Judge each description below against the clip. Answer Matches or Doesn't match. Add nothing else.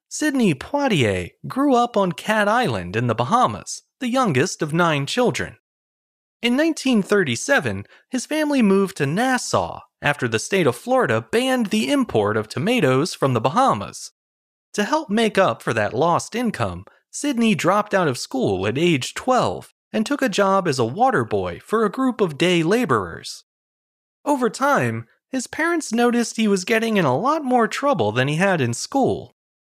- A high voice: Matches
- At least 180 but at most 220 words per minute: Doesn't match